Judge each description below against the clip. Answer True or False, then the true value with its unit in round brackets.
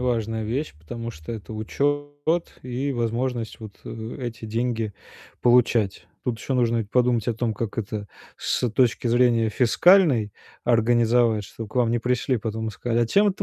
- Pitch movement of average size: False (1.9 semitones)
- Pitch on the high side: False (115 Hz)